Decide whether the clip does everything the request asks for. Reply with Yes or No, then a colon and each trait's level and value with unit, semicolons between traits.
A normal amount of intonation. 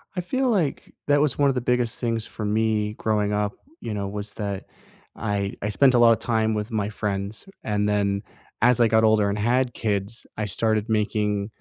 No: narrow, 2.3 semitones